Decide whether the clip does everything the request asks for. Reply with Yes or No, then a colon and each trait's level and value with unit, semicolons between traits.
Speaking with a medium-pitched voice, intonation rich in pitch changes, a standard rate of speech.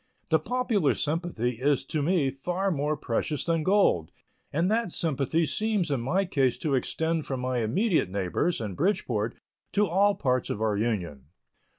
Yes: medium, 150 Hz; wide, 6.6 semitones; average, 165 wpm